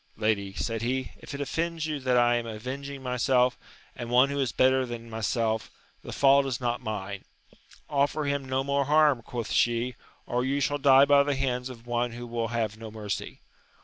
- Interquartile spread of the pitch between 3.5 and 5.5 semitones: No, average, 3.0 semitones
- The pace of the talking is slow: No, average, 195 wpm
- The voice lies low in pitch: Yes, low, 125 Hz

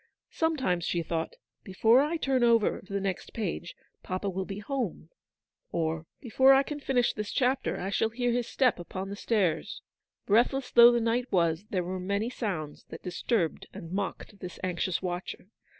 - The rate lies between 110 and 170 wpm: No, average, 180 wpm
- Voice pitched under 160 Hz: No, high, 200 Hz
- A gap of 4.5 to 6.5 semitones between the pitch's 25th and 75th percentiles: Yes, average, 5.2 semitones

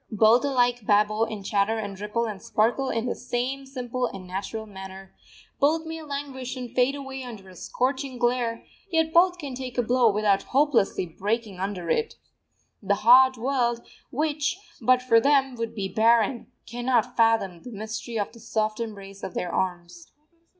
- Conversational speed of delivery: Yes, average, 170 wpm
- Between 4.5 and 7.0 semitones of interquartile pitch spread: No, average, 3.9 semitones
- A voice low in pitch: No, high, 235 Hz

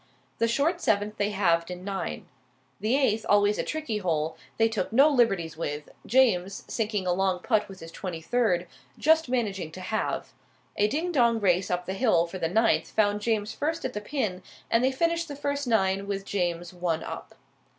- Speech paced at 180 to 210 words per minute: Yes, average, 190 wpm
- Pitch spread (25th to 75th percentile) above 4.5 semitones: Yes, average, 5.0 semitones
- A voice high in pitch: Yes, high, 205 Hz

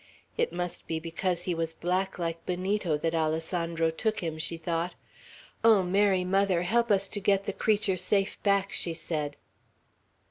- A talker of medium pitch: Yes, medium, 180 Hz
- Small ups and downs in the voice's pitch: No, average, 3.1 semitones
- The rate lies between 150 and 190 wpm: Yes, average, 165 wpm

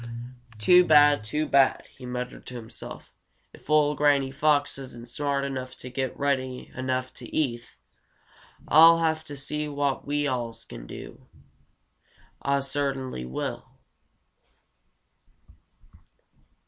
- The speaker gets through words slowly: Yes, slow, 120 wpm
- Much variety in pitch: No, narrow, 2.4 semitones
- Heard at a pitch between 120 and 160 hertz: Yes, medium, 140 Hz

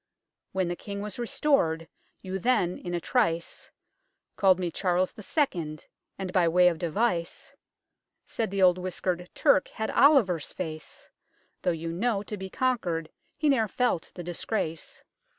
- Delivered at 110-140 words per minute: No, average, 150 wpm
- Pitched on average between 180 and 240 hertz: Yes, medium, 185 Hz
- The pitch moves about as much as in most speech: Yes, average, 3.8 semitones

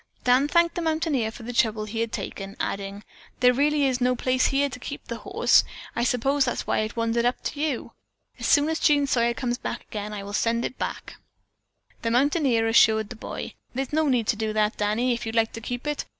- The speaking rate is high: Yes, fast, 220 wpm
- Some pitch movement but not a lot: Yes, average, 3.9 semitones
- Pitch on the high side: Yes, high, 245 Hz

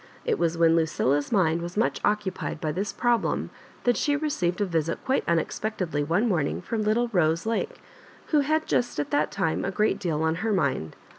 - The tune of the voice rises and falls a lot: Yes, wide, 5.7 semitones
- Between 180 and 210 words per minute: Yes, average, 195 wpm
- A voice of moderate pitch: Yes, medium, 180 Hz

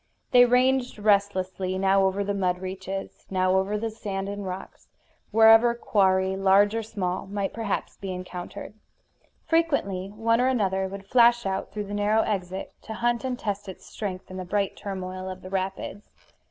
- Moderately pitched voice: No, high, 195 Hz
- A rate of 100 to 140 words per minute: No, average, 170 wpm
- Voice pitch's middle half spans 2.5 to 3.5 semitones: Yes, average, 2.8 semitones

